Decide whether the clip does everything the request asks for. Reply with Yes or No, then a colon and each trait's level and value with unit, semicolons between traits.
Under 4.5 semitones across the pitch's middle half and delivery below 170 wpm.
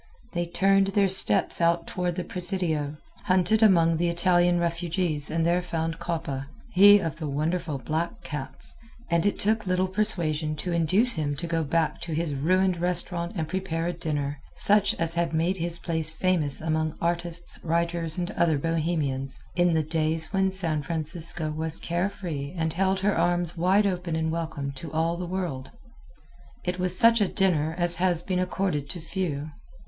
No: narrow, 2.4 semitones; average, 175 wpm